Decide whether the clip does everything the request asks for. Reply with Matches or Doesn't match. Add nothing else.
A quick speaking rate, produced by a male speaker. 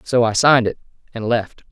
Matches